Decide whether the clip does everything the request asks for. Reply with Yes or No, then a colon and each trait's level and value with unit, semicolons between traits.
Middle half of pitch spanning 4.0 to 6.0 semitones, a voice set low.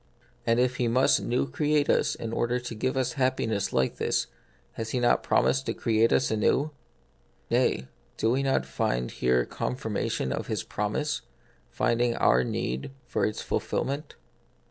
No: average, 3.6 semitones; low, 120 Hz